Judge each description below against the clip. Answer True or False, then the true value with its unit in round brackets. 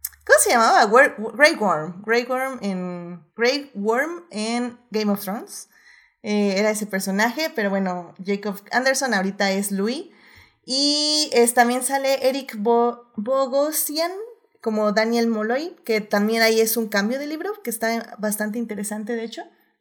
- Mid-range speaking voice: False (230 Hz)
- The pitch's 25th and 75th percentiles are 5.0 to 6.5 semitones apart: False (4.1 semitones)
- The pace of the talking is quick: False (140 wpm)